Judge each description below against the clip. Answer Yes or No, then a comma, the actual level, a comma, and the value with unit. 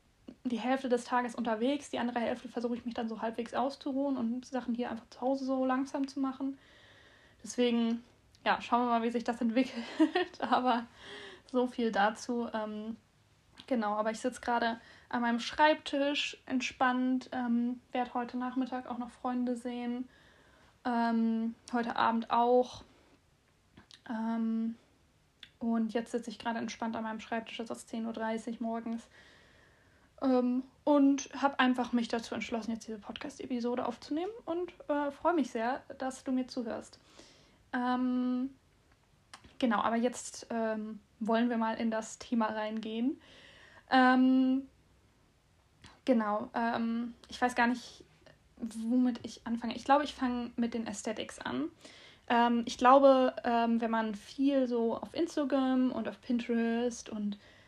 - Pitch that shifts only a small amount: Yes, narrow, 2.1 semitones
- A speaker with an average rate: Yes, average, 145 wpm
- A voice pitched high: Yes, high, 245 Hz